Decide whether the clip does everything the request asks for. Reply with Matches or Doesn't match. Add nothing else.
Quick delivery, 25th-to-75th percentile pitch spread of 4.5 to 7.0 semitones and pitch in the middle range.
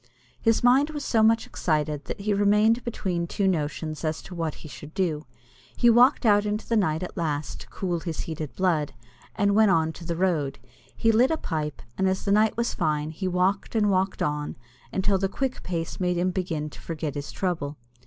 Matches